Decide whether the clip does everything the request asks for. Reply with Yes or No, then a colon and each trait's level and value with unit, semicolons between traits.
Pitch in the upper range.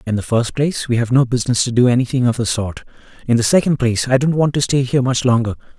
No: low, 125 Hz